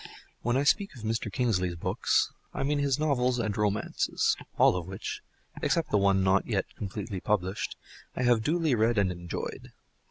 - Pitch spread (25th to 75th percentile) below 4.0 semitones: No, average, 4.8 semitones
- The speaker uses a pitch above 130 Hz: No, low, 110 Hz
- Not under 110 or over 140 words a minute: No, average, 170 wpm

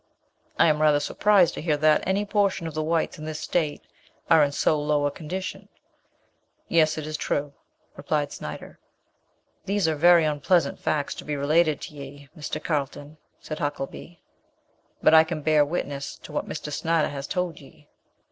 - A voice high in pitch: No, medium, 155 Hz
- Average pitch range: No, narrow, 2.3 semitones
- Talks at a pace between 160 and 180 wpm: Yes, average, 175 wpm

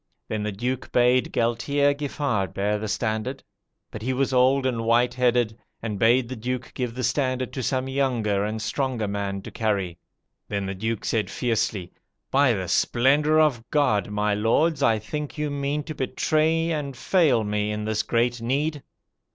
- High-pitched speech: No, low, 120 Hz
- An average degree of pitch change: Yes, average, 4.3 semitones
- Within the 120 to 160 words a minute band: No, average, 175 wpm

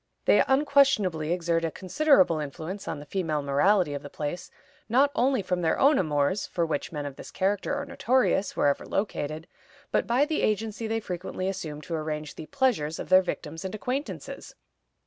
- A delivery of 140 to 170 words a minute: No, average, 180 wpm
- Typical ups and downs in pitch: No, wide, 6.6 semitones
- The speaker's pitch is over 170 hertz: Yes, medium, 185 Hz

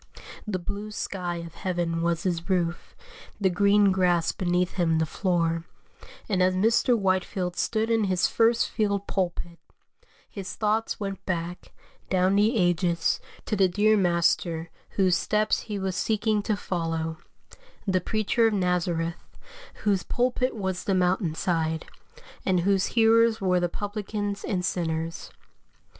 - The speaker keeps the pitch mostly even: No, average, 3.1 semitones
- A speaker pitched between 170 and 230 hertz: Yes, medium, 185 Hz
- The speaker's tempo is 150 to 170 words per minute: No, average, 140 wpm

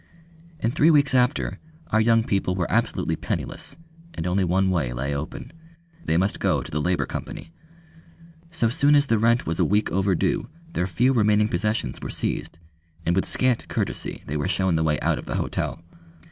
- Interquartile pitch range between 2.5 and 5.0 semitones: No, wide, 5.5 semitones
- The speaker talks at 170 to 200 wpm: Yes, average, 190 wpm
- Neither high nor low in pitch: No, very low, 95 Hz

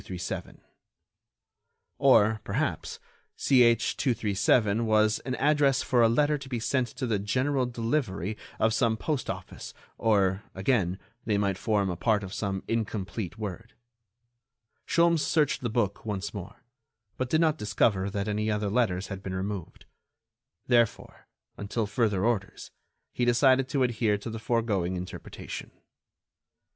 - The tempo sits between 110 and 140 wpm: Yes, slow, 135 wpm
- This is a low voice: Yes, low, 110 Hz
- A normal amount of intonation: Yes, average, 3.8 semitones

